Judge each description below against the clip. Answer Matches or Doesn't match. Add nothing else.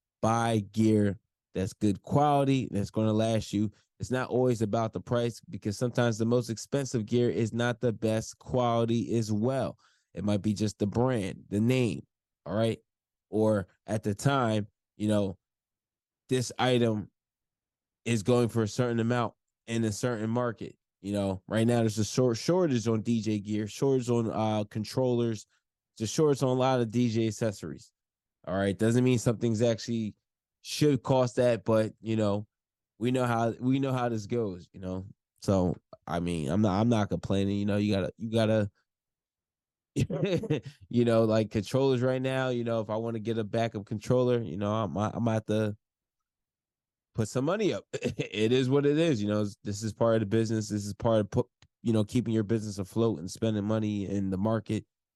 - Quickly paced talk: Doesn't match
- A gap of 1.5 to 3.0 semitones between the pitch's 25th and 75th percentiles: Matches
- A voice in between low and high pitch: Doesn't match